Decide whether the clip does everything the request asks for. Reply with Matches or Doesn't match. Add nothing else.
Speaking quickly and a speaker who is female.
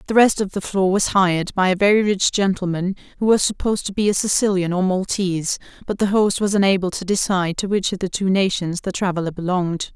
Matches